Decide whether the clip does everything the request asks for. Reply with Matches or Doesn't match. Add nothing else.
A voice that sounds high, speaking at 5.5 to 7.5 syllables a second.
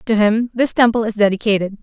Matches